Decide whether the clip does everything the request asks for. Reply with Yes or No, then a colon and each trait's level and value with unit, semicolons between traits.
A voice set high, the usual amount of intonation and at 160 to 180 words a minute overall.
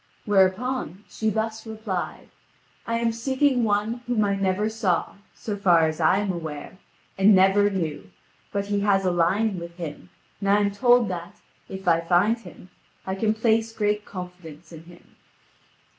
Yes: high, 200 Hz; average, 3.5 semitones; average, 165 wpm